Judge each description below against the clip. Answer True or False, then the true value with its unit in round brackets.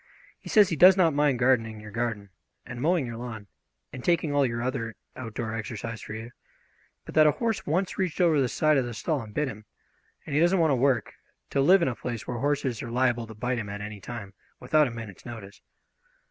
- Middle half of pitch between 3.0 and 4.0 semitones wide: False (4.8 semitones)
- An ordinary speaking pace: False (230 wpm)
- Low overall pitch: True (125 Hz)